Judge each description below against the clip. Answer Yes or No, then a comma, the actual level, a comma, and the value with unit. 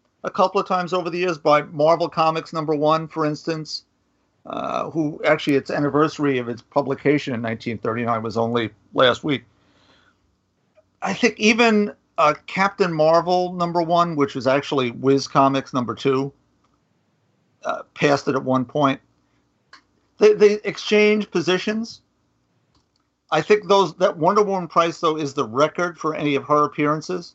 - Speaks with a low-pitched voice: No, medium, 155 Hz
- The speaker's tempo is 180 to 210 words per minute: No, average, 150 wpm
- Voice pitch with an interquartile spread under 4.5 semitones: No, average, 4.9 semitones